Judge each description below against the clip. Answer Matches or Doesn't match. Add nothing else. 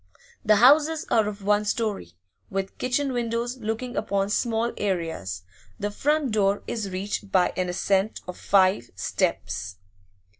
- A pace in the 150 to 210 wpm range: Doesn't match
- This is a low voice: Doesn't match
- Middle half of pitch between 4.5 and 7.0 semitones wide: Doesn't match